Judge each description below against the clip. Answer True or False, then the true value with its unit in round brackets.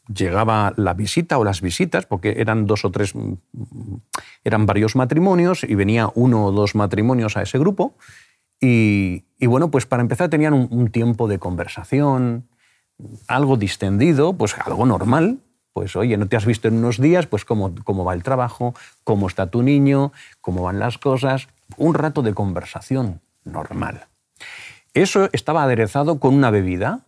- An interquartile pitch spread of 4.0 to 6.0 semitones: True (4.5 semitones)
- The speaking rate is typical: True (165 wpm)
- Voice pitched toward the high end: False (115 Hz)